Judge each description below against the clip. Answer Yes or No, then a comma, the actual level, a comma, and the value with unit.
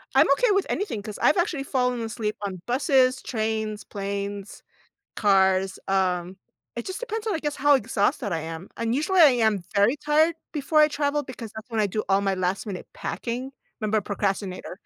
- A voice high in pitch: Yes, high, 220 Hz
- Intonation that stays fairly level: No, wide, 6.4 semitones